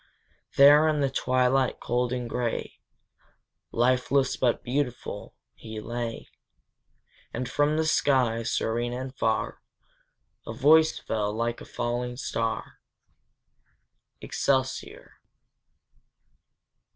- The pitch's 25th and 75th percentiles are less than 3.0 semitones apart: Yes, narrow, 2.4 semitones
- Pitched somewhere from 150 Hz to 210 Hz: No, low, 125 Hz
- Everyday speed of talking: No, slow, 95 wpm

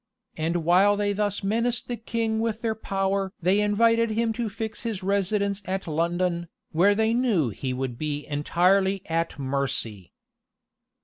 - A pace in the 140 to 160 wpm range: Yes, average, 150 wpm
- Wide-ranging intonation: No, average, 4.8 semitones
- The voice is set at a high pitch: Yes, high, 195 Hz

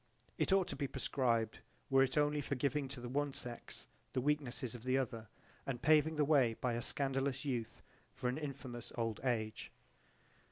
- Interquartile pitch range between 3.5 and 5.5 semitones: No, average, 3.0 semitones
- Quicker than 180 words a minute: Yes, average, 190 wpm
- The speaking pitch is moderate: No, low, 130 Hz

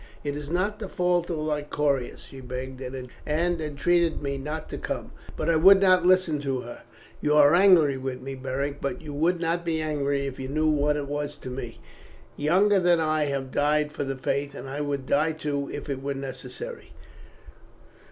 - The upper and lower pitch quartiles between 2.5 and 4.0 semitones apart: Yes, average, 3.3 semitones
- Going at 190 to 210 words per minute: Yes, average, 195 wpm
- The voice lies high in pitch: No, medium, 150 Hz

